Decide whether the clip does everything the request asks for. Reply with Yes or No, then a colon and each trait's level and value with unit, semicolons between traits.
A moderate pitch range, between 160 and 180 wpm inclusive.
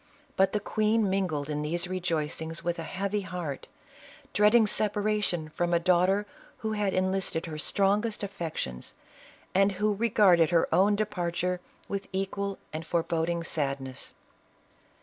No: average, 3.5 semitones; average, 140 wpm